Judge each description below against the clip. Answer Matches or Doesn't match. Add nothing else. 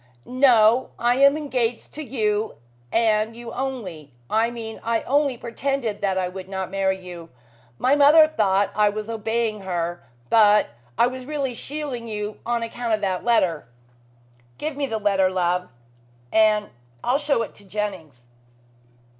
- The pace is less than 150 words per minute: Doesn't match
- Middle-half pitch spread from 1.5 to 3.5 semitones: Doesn't match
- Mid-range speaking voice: Doesn't match